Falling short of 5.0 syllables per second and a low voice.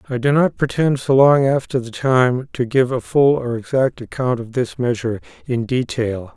Yes: 4.8 syllables/s; low, 125 Hz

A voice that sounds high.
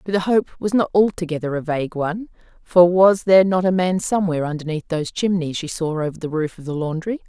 No: medium, 175 Hz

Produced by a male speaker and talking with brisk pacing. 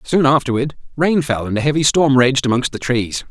Yes: male; fast, 220 wpm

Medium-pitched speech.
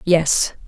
Yes: medium, 165 Hz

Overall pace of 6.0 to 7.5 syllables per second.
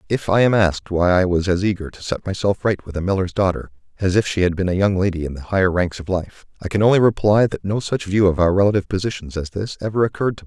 Yes: 6.7 syllables/s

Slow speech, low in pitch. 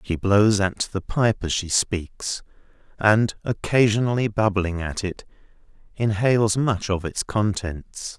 Yes: slow, 130 wpm; low, 105 Hz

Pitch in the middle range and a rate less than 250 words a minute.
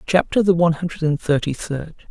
Yes: medium, 165 Hz; average, 200 wpm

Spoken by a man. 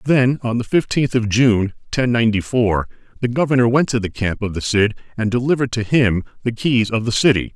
Yes: male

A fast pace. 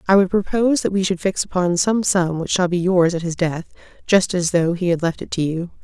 Yes: fast, 255 wpm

